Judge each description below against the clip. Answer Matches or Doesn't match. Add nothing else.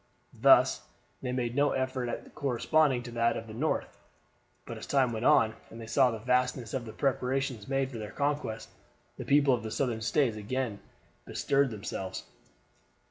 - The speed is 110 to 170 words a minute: Doesn't match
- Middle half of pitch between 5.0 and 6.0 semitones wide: Doesn't match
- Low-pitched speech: Matches